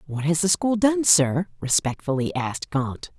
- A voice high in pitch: No, medium, 160 Hz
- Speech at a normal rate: Yes, average, 170 wpm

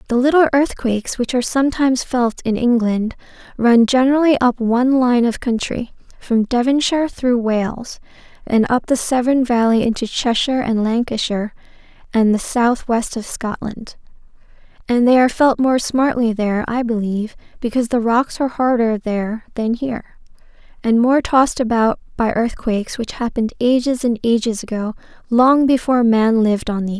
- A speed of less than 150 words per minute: No, average, 155 wpm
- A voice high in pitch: Yes, high, 240 Hz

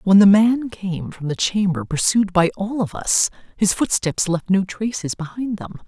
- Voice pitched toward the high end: Yes, high, 195 Hz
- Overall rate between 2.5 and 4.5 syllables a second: Yes, 4.4 syllables/s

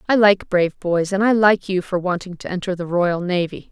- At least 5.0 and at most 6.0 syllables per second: Yes, 5.4 syllables/s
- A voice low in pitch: No, medium, 185 Hz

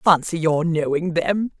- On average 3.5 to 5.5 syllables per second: Yes, 4.1 syllables/s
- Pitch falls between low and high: Yes, medium, 165 Hz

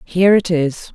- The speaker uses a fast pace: No, average, 190 wpm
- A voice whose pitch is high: No, medium, 170 Hz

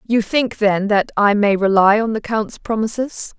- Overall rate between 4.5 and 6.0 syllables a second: No, 4.1 syllables/s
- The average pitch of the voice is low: No, high, 215 Hz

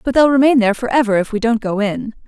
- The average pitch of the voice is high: Yes, high, 235 Hz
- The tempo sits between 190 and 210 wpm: No, fast, 290 wpm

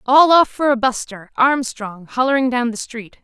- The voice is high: Yes, very high, 250 Hz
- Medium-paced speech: Yes, average, 185 wpm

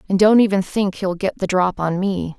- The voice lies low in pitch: No, high, 190 Hz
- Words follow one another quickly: Yes, fast, 250 wpm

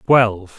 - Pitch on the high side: No, low, 110 Hz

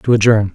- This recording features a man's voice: Yes, male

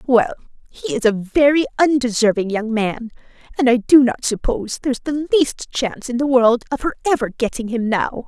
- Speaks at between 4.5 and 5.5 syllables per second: Yes, 5.3 syllables/s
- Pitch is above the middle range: Yes, high, 245 Hz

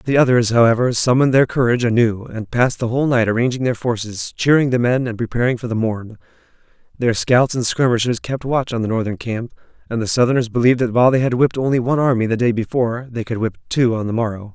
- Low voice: Yes, low, 120 Hz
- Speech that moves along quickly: Yes, fast, 225 wpm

